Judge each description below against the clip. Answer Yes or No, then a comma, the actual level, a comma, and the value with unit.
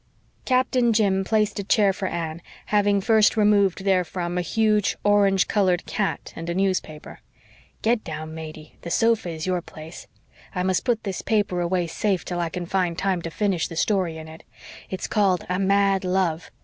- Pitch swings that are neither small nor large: Yes, average, 3.1 semitones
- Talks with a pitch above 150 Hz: Yes, high, 190 Hz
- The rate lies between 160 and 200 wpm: Yes, average, 180 wpm